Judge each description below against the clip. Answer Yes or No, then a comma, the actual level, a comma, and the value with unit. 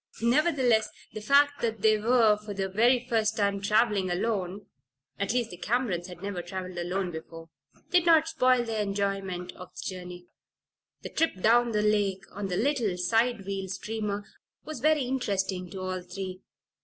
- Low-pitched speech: No, high, 205 Hz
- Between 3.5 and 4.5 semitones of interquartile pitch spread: Yes, average, 4.1 semitones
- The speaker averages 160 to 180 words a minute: Yes, average, 170 wpm